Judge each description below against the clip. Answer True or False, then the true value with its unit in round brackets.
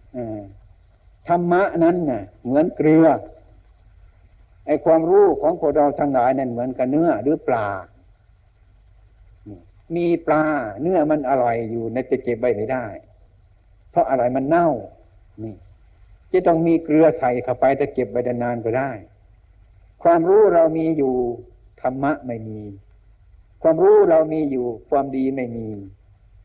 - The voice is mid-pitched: False (120 Hz)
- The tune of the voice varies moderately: False (7.3 semitones)